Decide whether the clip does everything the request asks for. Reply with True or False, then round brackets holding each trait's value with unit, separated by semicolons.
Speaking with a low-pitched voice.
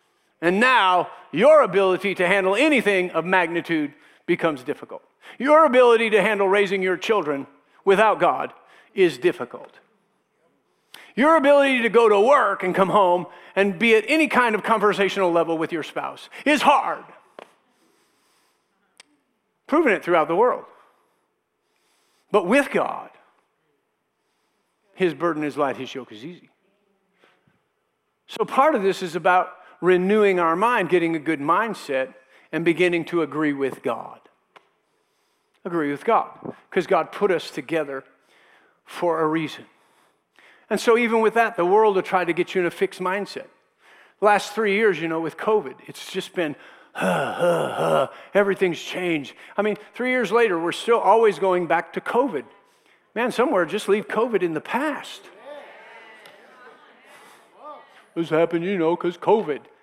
False (195 Hz)